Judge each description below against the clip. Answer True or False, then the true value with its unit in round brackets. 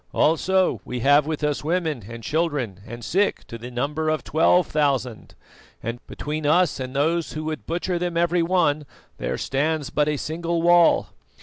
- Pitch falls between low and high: True (155 Hz)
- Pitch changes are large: False (3.3 semitones)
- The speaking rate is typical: True (175 wpm)